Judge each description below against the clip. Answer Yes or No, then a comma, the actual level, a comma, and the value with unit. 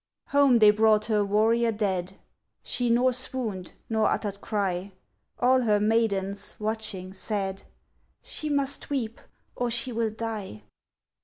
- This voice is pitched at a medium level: No, high, 220 Hz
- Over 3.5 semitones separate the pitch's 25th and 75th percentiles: No, average, 2.9 semitones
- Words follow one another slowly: Yes, slow, 130 wpm